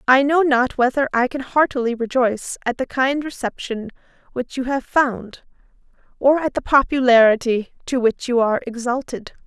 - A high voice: Yes, very high, 255 Hz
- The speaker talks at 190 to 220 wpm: No, average, 160 wpm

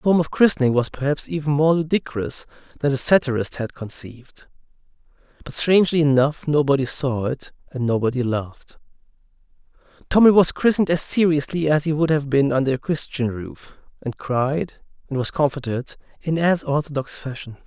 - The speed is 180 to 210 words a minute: No, average, 155 wpm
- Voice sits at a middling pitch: Yes, medium, 145 Hz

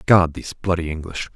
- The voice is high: No, very low, 85 Hz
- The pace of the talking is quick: No, average, 175 wpm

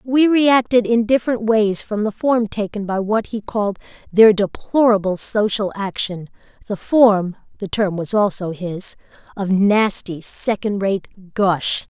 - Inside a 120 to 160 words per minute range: Yes, average, 140 wpm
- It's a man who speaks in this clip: No, female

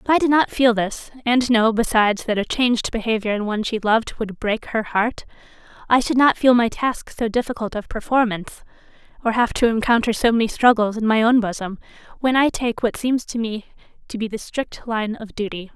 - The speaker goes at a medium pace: No, fast, 215 wpm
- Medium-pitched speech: No, high, 230 Hz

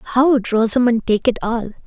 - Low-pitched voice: No, high, 235 Hz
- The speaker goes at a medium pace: Yes, average, 195 wpm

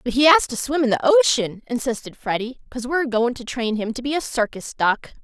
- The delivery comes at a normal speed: No, fast, 240 wpm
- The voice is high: Yes, very high, 250 Hz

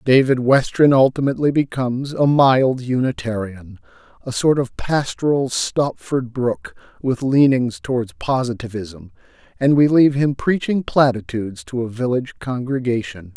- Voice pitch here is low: Yes, low, 125 Hz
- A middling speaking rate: No, slow, 120 wpm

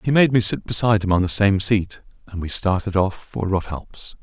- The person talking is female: No, male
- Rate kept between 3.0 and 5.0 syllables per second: No, 5.2 syllables/s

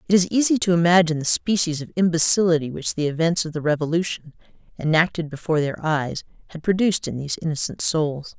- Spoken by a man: No, female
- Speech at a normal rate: Yes, average, 180 wpm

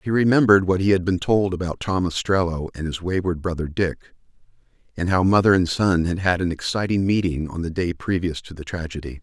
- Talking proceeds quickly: Yes, fast, 210 wpm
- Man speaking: Yes, male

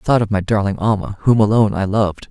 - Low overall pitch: Yes, low, 105 Hz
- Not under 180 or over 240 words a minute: No, fast, 260 wpm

